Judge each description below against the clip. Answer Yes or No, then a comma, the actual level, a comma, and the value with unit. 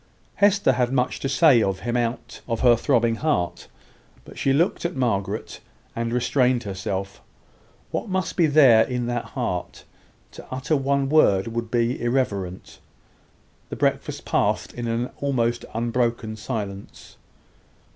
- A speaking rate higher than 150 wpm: No, average, 140 wpm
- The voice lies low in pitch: Yes, low, 120 Hz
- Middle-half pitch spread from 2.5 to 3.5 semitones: Yes, average, 3.1 semitones